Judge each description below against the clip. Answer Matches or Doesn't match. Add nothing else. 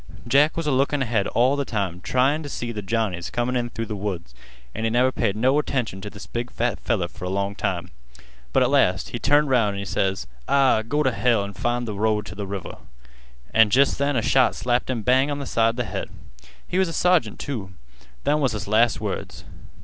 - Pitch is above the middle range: Doesn't match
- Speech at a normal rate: Doesn't match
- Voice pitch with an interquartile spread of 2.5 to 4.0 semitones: Doesn't match